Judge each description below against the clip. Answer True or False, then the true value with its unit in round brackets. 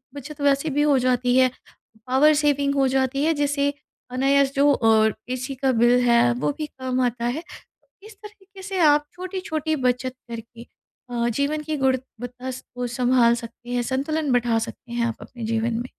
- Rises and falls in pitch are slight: False (3.2 semitones)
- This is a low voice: False (260 Hz)